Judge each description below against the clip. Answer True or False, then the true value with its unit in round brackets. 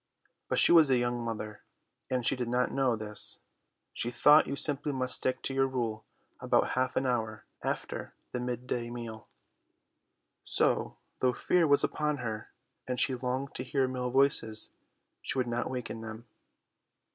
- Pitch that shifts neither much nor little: False (2.2 semitones)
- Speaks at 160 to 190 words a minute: True (170 wpm)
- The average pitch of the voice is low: True (125 Hz)